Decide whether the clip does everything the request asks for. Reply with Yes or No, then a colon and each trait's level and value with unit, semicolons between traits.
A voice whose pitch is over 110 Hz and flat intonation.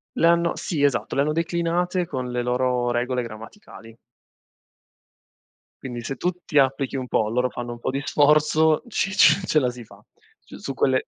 No: low, 135 Hz; average, 4.4 semitones